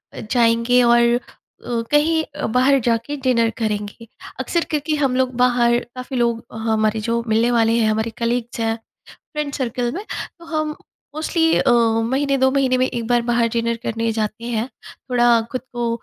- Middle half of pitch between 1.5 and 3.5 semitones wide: Yes, narrow, 2.4 semitones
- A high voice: Yes, high, 240 Hz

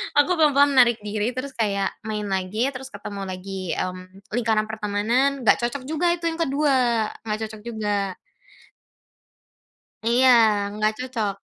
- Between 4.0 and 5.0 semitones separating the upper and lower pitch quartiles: Yes, average, 4.3 semitones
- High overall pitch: Yes, high, 220 Hz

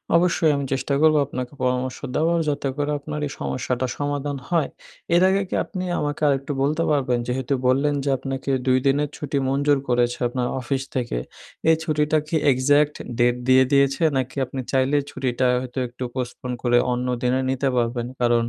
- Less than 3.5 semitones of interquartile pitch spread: Yes, narrow, 2.5 semitones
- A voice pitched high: No, low, 135 Hz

